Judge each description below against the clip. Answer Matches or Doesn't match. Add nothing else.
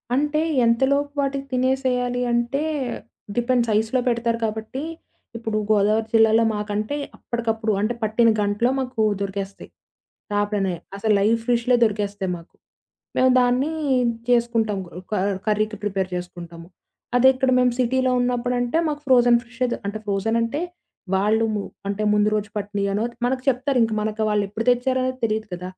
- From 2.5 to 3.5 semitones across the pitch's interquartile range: Matches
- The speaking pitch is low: Doesn't match